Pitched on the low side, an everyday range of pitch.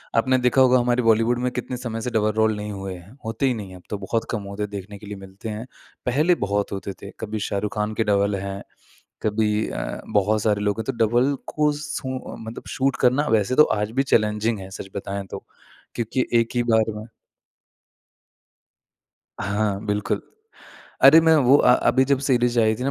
Yes: low, 110 Hz; average, 3.4 semitones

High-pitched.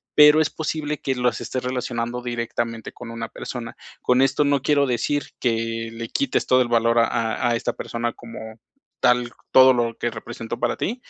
No: low, 120 Hz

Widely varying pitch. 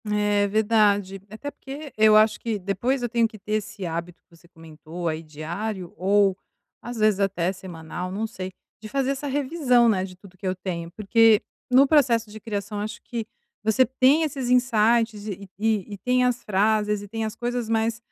No: average, 3.5 semitones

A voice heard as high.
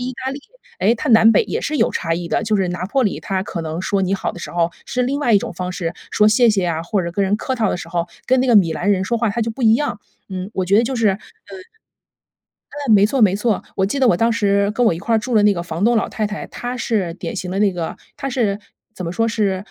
Yes: high, 205 Hz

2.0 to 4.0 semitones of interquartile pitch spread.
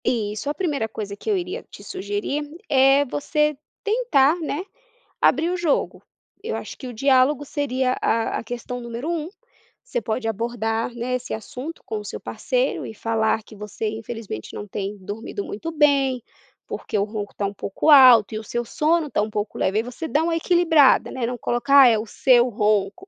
No: wide, 5.5 semitones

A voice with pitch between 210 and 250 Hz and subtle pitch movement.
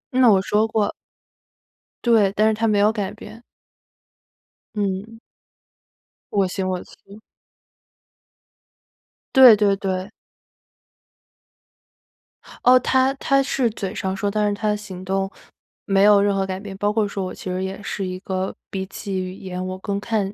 No: high, 200 Hz; narrow, 2.0 semitones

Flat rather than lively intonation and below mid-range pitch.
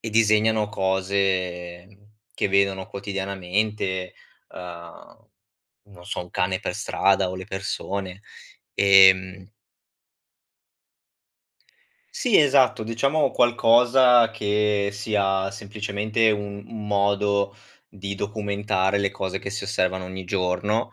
Yes: narrow, 2.0 semitones; low, 100 Hz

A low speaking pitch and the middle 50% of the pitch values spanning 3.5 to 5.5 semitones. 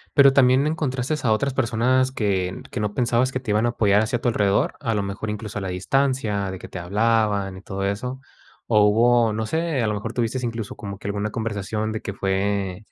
Yes: low, 110 Hz; average, 3.8 semitones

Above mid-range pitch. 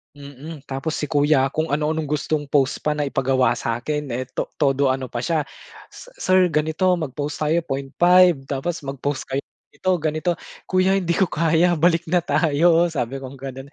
No: medium, 150 Hz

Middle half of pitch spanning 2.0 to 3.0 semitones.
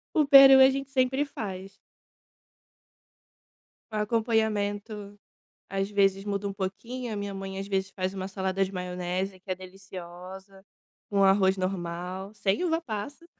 Yes: narrow, 2.5 semitones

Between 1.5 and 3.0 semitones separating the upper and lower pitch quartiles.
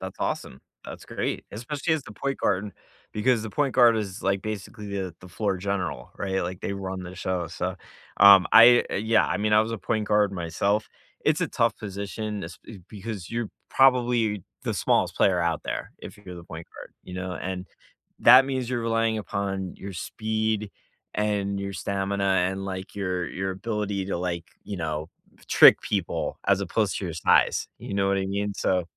Yes: average, 2.7 semitones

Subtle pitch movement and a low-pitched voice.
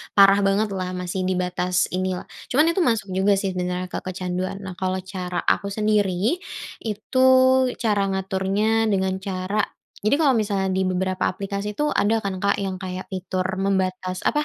No: narrow, 1.5 semitones; high, 190 Hz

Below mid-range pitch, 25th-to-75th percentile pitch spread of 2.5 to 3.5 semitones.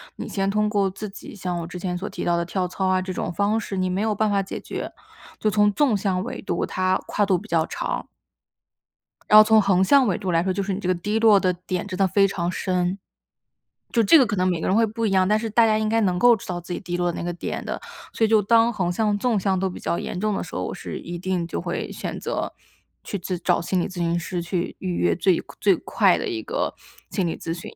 No: high, 190 Hz; average, 2.9 semitones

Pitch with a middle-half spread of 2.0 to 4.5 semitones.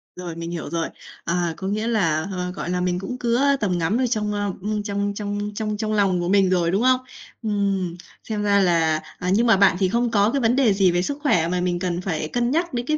Yes: average, 3.6 semitones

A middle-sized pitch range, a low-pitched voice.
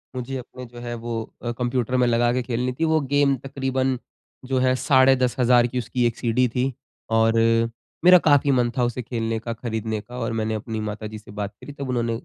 No: narrow, 2.2 semitones; low, 125 Hz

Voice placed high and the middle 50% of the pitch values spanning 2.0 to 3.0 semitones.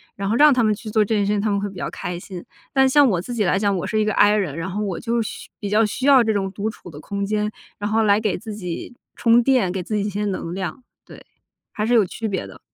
Yes: high, 210 Hz; narrow, 2.4 semitones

